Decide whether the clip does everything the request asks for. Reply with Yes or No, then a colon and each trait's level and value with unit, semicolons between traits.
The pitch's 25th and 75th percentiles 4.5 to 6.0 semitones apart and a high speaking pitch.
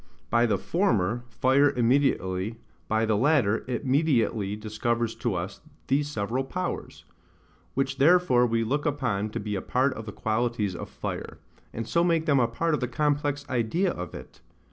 No: average, 4.8 semitones; low, 120 Hz